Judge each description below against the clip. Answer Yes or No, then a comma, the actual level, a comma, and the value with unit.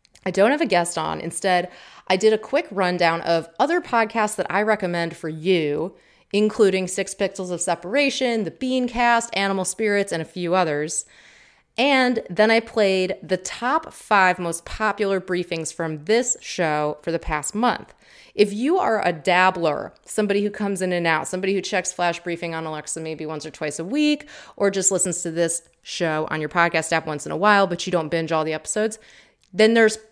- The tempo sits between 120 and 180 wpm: No, average, 195 wpm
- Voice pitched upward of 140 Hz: Yes, medium, 185 Hz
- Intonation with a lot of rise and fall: No, average, 4.2 semitones